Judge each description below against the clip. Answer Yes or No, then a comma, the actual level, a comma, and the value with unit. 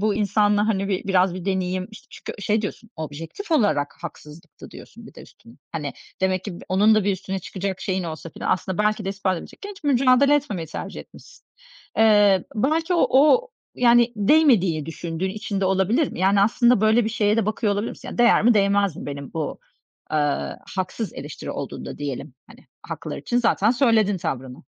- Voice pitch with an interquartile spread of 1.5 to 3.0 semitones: No, average, 3.8 semitones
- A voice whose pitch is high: Yes, high, 200 Hz